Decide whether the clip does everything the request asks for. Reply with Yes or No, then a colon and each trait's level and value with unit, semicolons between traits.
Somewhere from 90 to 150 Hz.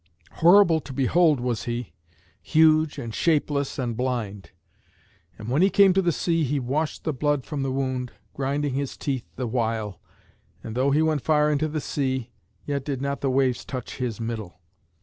Yes: low, 135 Hz